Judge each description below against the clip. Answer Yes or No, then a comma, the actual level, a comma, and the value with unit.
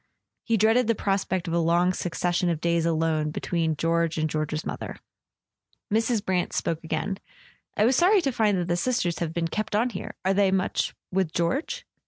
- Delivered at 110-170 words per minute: No, average, 190 wpm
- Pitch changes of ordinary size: Yes, average, 4.1 semitones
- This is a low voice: No, medium, 180 Hz